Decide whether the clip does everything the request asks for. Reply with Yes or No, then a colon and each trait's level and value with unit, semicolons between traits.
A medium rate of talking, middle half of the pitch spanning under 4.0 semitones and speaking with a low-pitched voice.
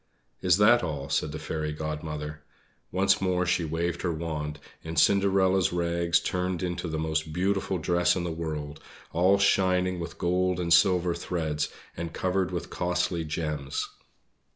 Yes: average, 155 wpm; average, 2.7 semitones; very low, 85 Hz